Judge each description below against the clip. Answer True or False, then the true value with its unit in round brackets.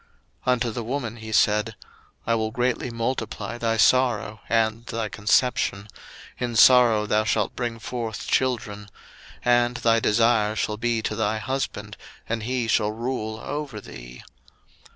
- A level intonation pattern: True (2.1 semitones)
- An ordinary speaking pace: True (145 wpm)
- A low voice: True (115 Hz)